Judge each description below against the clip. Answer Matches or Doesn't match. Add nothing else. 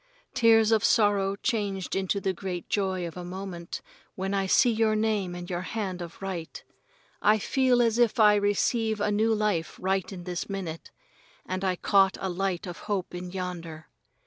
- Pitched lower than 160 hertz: Doesn't match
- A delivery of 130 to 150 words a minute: Doesn't match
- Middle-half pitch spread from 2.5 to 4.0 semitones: Matches